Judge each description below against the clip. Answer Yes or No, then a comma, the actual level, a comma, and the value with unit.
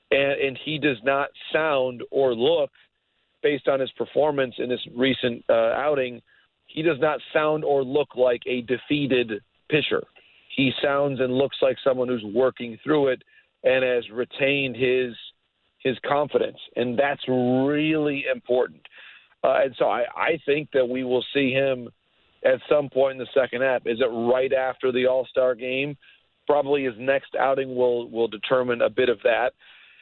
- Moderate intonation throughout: No, narrow, 2.1 semitones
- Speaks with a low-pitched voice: Yes, low, 130 Hz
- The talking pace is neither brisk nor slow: Yes, average, 170 wpm